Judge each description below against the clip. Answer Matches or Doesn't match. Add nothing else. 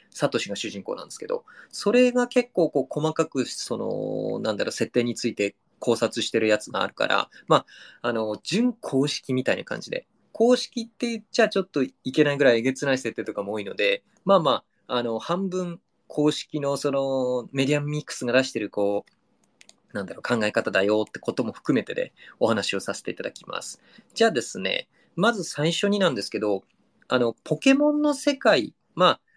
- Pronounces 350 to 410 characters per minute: Matches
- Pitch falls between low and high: Matches